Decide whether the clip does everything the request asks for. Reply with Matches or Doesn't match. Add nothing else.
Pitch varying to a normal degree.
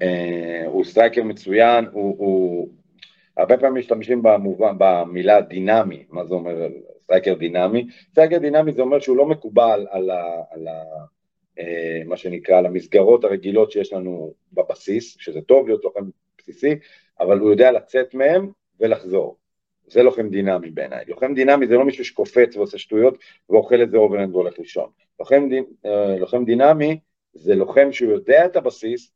Doesn't match